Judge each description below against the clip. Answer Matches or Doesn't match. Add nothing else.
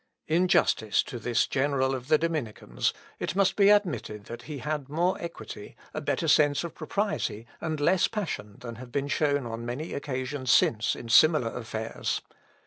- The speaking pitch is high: Doesn't match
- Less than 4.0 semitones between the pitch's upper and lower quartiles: Doesn't match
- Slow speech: Doesn't match